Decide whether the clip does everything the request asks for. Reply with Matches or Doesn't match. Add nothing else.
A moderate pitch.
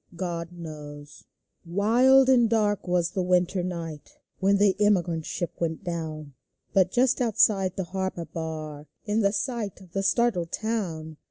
Matches